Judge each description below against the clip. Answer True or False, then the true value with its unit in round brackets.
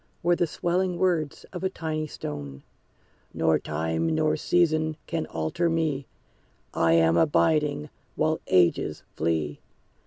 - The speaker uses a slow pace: True (125 wpm)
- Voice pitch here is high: False (150 Hz)